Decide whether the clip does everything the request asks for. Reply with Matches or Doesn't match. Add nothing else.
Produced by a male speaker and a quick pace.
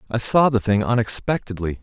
Doesn't match